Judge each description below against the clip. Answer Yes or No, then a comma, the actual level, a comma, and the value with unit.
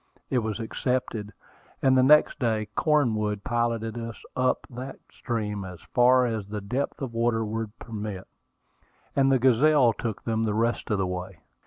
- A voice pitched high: No, low, 115 Hz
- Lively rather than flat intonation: No, average, 3.1 semitones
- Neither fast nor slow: Yes, average, 165 wpm